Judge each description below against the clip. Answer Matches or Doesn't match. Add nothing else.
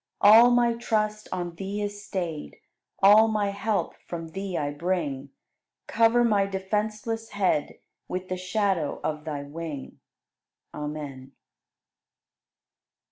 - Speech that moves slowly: Matches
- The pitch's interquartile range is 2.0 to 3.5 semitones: Doesn't match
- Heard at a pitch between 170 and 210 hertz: Matches